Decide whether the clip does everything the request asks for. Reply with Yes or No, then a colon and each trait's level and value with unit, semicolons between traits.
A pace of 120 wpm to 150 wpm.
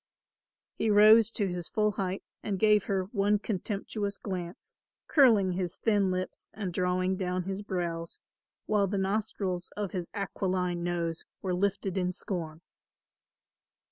Yes: average, 140 wpm